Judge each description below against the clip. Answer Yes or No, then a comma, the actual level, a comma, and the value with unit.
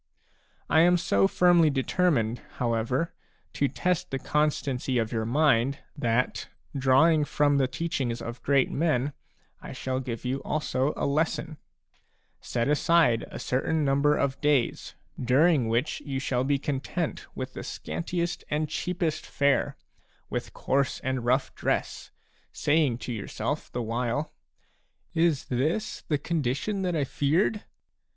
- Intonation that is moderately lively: Yes, average, 3.9 semitones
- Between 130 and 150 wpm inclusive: Yes, average, 140 wpm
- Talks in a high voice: No, medium, 140 Hz